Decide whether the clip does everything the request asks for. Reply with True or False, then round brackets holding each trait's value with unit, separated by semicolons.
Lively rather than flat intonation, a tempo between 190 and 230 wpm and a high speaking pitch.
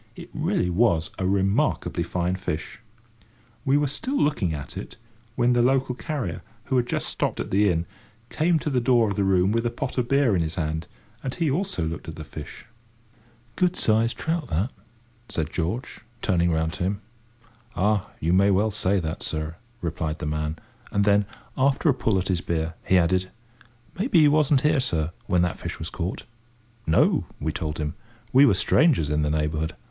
False (7.7 semitones; 195 wpm; 95 Hz)